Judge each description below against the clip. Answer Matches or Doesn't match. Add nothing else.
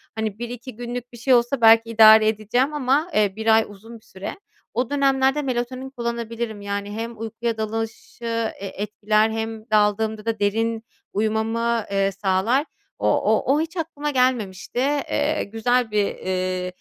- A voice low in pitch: Doesn't match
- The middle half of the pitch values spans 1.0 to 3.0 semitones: Matches